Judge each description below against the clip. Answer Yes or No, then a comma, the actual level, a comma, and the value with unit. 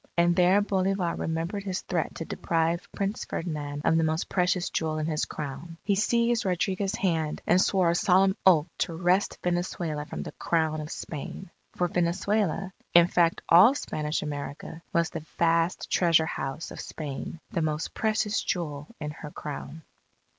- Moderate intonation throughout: Yes, average, 3.0 semitones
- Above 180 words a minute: No, average, 165 wpm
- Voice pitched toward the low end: No, medium, 170 Hz